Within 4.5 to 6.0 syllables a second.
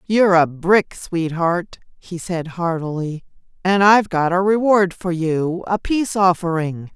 No: 4.2 syllables/s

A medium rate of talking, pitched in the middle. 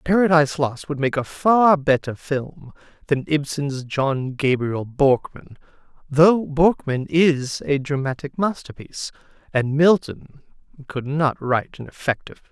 No: slow, 130 wpm; medium, 145 Hz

